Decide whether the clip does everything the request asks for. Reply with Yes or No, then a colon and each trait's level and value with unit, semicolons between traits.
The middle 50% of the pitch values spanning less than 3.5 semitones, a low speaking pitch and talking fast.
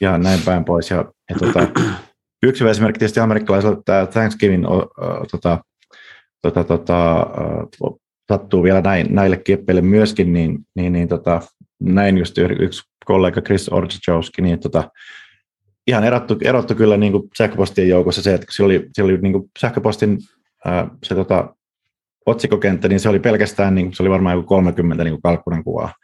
Yes: average, 2.9 semitones; very low, 95 Hz; fast, 160 wpm